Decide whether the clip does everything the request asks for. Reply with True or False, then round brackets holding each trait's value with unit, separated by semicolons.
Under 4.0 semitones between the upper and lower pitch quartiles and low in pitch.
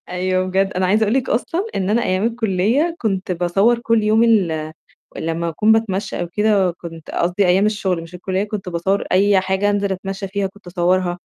False (2.8 semitones; 195 Hz)